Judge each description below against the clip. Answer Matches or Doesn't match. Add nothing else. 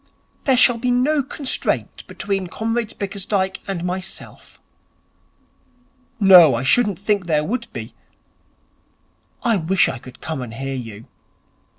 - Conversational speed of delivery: Doesn't match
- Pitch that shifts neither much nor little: Doesn't match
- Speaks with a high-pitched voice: Matches